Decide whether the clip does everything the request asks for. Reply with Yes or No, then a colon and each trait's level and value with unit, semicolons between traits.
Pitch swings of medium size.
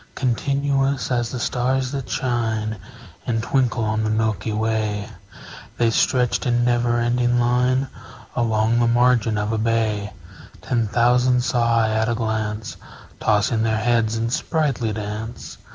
No: narrow, 2.0 semitones